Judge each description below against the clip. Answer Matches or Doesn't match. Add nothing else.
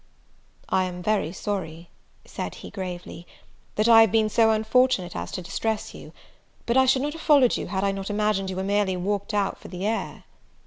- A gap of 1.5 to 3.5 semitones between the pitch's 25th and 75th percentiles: Matches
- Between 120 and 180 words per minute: Doesn't match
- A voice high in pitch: Matches